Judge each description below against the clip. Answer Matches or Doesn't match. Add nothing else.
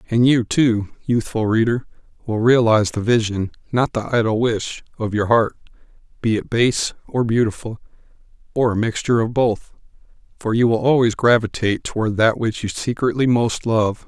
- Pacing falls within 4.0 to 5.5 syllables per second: Matches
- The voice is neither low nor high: Doesn't match